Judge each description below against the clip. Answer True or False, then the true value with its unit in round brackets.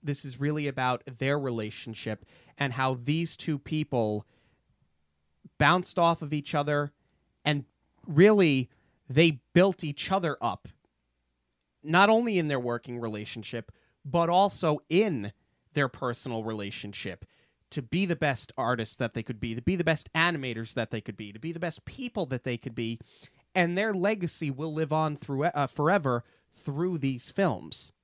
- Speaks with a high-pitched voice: False (140 Hz)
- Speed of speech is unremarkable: True (160 wpm)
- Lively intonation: True (5.9 semitones)